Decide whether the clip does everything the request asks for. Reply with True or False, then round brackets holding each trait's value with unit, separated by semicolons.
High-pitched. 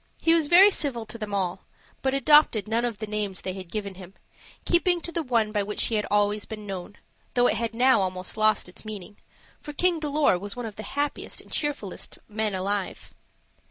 True (215 Hz)